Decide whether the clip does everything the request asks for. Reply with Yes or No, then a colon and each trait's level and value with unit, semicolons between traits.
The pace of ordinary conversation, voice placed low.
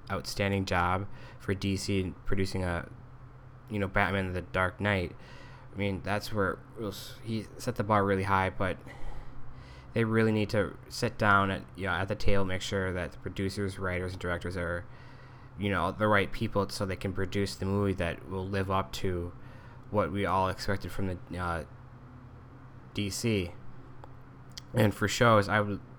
Yes: average, 170 wpm; low, 100 Hz